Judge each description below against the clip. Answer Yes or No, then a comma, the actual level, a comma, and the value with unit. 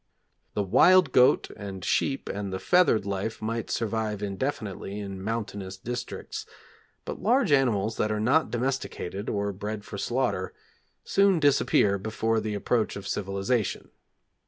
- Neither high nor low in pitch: No, low, 110 Hz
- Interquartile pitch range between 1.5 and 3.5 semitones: No, average, 4.0 semitones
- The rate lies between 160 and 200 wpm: No, slow, 135 wpm